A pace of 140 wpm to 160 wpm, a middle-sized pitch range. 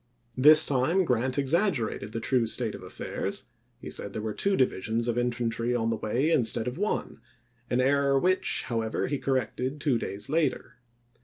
No: average, 175 wpm; average, 3.7 semitones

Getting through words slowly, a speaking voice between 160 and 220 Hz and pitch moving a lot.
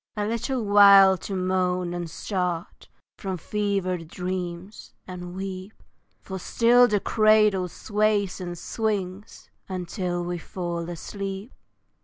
No: slow, 115 wpm; high, 190 Hz; narrow, 2.5 semitones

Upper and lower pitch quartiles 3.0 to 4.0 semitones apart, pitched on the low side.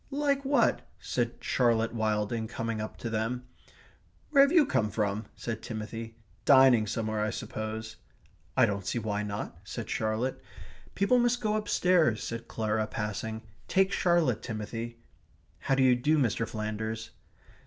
Yes: average, 3.5 semitones; low, 115 Hz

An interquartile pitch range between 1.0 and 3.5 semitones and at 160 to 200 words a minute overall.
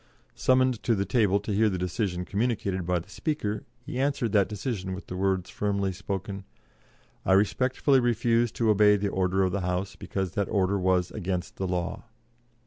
Yes: average, 3.0 semitones; average, 180 wpm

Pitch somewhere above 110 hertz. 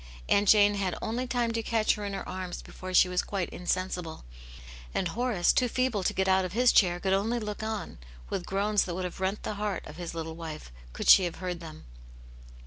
Yes: high, 190 Hz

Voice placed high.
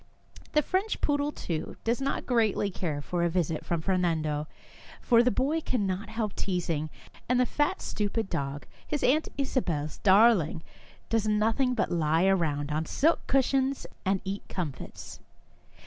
Yes: high, 200 Hz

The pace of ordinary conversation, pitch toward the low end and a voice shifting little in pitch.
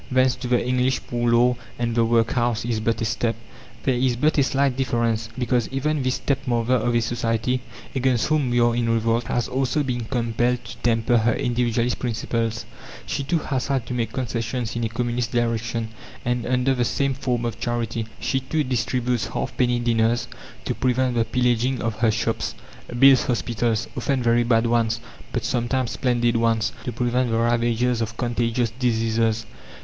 Yes: average, 175 wpm; low, 120 Hz; narrow, 1.6 semitones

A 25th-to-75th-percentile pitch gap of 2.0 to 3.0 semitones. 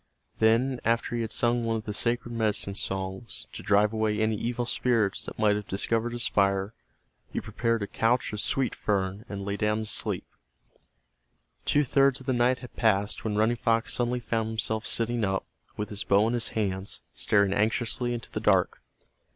Yes: narrow, 2.5 semitones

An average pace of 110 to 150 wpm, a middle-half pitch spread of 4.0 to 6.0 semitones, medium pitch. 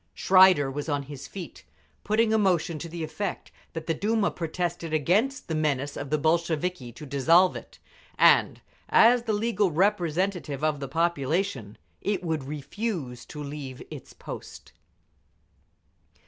Yes: average, 145 wpm; average, 4.7 semitones; medium, 165 Hz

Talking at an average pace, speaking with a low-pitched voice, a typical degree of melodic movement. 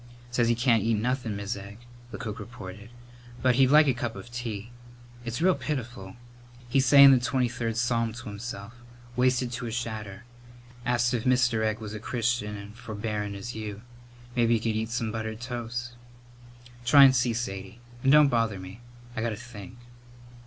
No: average, 180 wpm; low, 115 Hz; narrow, 2.3 semitones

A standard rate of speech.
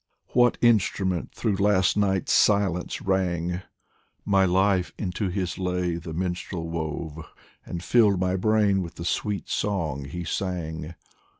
No: slow, 130 wpm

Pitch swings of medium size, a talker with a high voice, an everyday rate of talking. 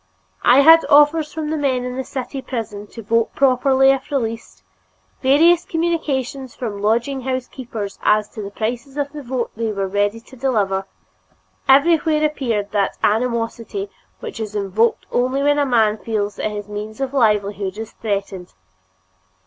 Yes: average, 4.7 semitones; high, 245 Hz; average, 160 wpm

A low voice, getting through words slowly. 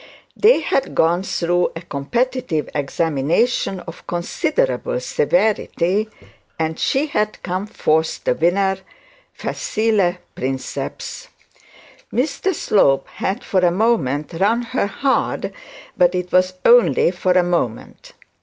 No: medium, 180 Hz; slow, 115 wpm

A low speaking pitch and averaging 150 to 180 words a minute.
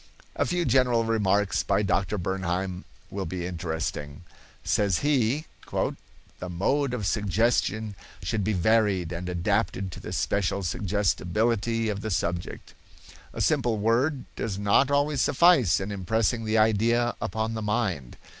No: low, 105 Hz; slow, 135 wpm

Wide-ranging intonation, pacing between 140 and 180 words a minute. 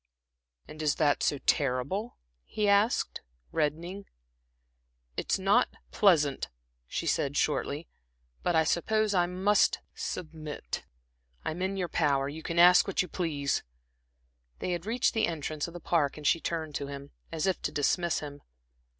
No: average, 4.2 semitones; average, 150 wpm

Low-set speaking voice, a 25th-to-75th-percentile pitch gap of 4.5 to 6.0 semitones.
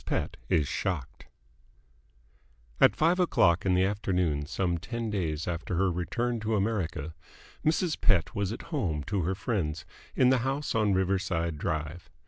Yes: very low, 95 Hz; average, 5.3 semitones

